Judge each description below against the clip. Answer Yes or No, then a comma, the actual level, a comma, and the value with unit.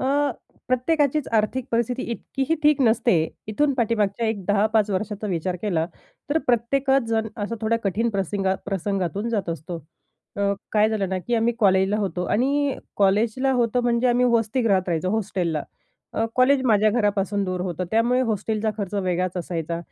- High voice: Yes, high, 215 Hz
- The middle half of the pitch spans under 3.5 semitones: No, average, 3.8 semitones